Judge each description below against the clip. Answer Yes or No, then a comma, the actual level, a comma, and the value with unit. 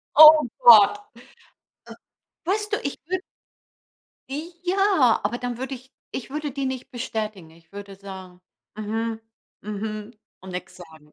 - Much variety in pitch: Yes, wide, 6.1 semitones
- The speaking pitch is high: Yes, high, 230 Hz